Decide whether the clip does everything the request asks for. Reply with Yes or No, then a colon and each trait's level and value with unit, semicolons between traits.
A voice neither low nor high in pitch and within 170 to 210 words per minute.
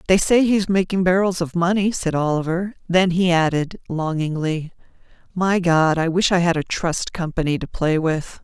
Yes: medium, 175 Hz; average, 180 wpm